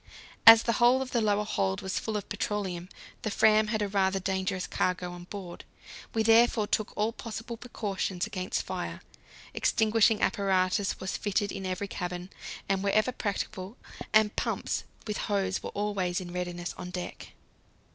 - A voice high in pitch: Yes, high, 200 Hz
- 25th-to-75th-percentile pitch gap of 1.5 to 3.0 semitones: Yes, average, 2.7 semitones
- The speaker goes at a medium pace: Yes, average, 160 wpm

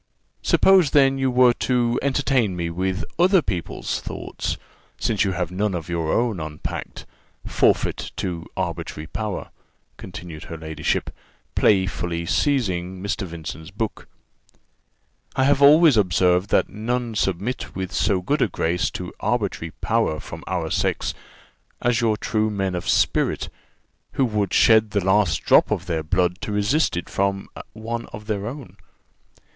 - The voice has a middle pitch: No, low, 100 Hz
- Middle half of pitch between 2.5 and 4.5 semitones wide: No, average, 5.0 semitones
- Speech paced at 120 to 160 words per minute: Yes, average, 145 wpm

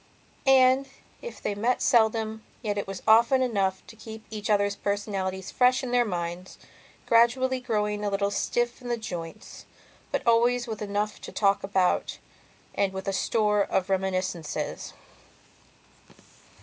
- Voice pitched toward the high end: Yes, high, 210 Hz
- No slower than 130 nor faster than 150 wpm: Yes, average, 145 wpm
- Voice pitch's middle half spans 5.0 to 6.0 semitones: No, average, 3.5 semitones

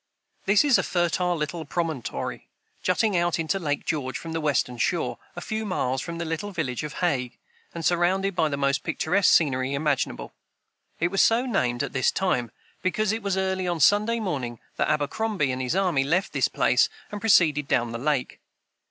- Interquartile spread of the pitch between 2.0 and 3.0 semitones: No, wide, 5.4 semitones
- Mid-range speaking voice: Yes, medium, 165 Hz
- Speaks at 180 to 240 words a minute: Yes, average, 185 wpm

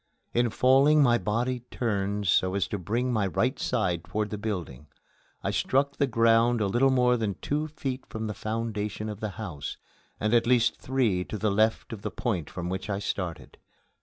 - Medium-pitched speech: No, low, 110 Hz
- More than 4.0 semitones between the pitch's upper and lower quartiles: No, average, 3.7 semitones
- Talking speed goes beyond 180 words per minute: Yes, average, 195 wpm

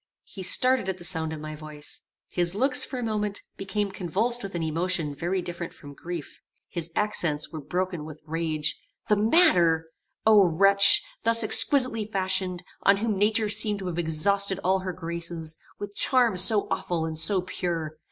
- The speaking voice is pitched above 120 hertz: Yes, medium, 185 Hz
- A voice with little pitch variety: No, average, 4.2 semitones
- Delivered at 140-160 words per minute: No, average, 170 wpm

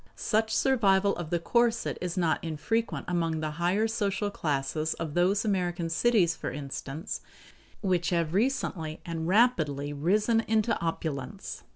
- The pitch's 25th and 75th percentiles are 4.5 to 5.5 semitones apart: Yes, average, 5.0 semitones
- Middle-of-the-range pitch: Yes, medium, 175 Hz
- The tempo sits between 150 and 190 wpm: No, average, 140 wpm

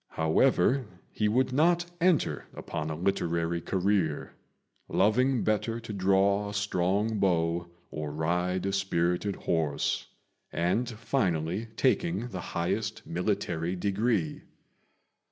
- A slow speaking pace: Yes, slow, 110 wpm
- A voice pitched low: Yes, very low, 95 Hz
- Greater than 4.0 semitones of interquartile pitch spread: Yes, average, 4.7 semitones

